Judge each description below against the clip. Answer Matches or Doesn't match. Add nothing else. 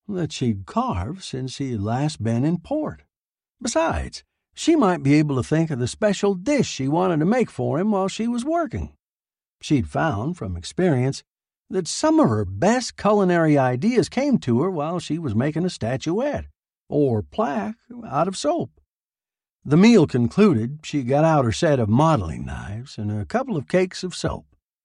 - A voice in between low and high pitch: Matches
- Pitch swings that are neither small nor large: Doesn't match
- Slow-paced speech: Doesn't match